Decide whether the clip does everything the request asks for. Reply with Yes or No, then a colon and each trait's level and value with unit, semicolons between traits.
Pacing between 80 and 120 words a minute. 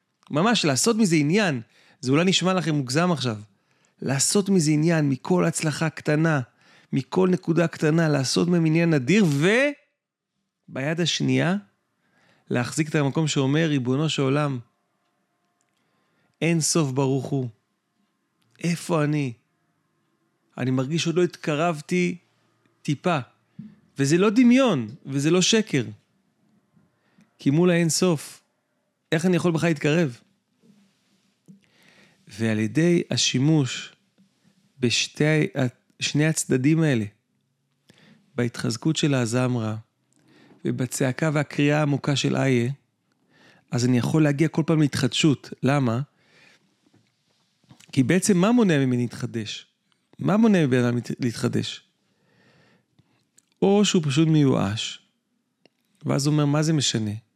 Yes: average, 110 wpm